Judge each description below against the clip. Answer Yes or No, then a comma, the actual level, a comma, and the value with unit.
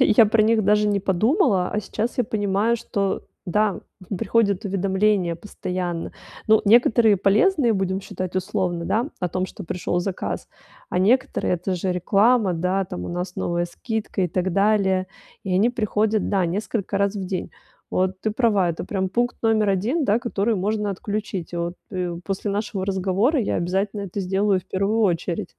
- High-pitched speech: Yes, high, 200 Hz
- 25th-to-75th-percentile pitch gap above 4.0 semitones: No, average, 2.7 semitones